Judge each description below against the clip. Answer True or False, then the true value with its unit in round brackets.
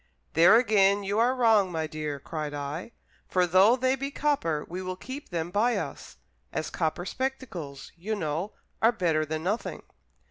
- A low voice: False (185 Hz)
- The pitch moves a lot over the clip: True (6.4 semitones)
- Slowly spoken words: False (170 wpm)